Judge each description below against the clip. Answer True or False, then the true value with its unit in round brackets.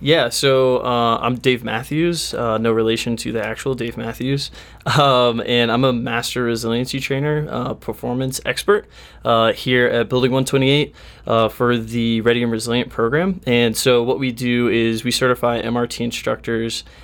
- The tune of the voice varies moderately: False (2.2 semitones)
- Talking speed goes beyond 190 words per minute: False (160 wpm)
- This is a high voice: False (120 Hz)